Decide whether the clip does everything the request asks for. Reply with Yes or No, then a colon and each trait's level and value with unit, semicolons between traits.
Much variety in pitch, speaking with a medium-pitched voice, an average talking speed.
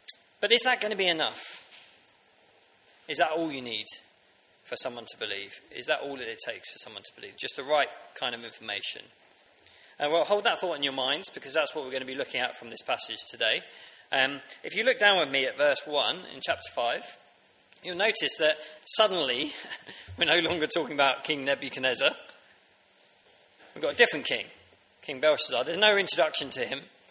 Yes: wide, 6.7 semitones; medium, 155 Hz; average, 195 wpm